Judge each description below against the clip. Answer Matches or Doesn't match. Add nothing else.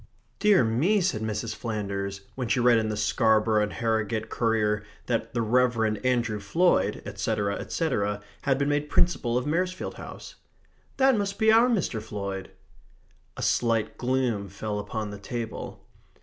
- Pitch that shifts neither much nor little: Matches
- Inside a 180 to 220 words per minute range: Doesn't match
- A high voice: Doesn't match